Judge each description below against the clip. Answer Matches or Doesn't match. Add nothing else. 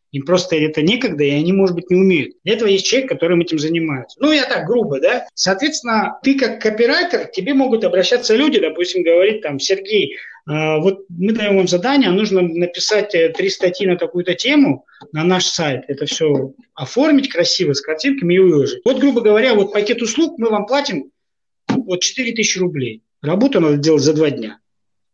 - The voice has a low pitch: Doesn't match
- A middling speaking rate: Doesn't match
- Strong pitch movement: Matches